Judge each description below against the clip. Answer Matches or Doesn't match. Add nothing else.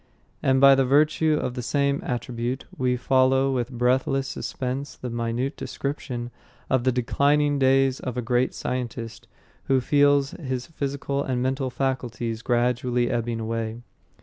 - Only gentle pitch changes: Matches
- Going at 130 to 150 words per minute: Matches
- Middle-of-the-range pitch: Doesn't match